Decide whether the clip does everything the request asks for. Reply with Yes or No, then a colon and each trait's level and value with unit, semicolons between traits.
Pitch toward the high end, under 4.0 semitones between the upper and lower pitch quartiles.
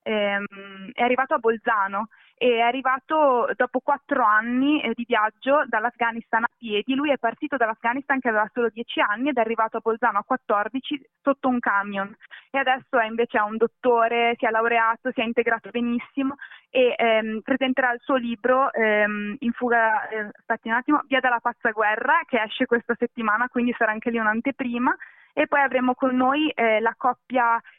Yes: high, 235 Hz; average, 2.7 semitones